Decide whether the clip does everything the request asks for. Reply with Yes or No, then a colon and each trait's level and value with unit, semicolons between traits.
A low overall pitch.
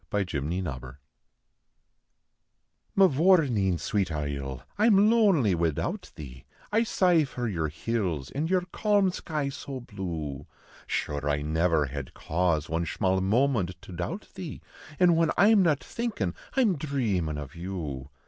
Yes: very low, 95 Hz